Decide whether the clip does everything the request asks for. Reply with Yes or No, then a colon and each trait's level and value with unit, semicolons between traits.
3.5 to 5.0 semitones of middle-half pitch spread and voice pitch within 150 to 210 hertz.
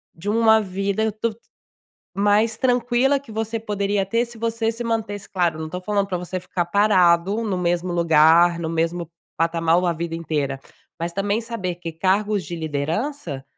Yes: average, 4.5 semitones; high, 190 Hz